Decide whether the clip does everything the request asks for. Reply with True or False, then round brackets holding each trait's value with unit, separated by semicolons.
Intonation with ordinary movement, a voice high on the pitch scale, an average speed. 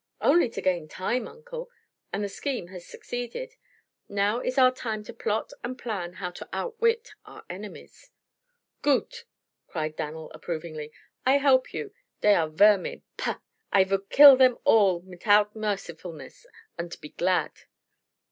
False (6.5 semitones; 205 Hz; 145 wpm)